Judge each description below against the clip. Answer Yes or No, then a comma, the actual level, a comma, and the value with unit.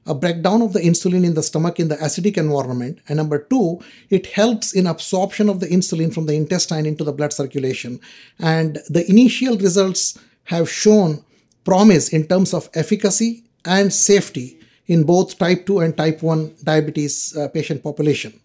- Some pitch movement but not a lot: Yes, average, 4.0 semitones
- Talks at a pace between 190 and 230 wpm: No, average, 170 wpm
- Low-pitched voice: No, medium, 170 Hz